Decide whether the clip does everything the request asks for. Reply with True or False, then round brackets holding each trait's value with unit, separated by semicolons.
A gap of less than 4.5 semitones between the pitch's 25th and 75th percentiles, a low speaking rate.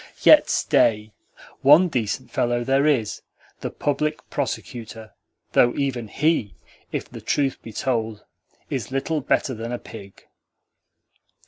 True (3.8 semitones; 125 wpm)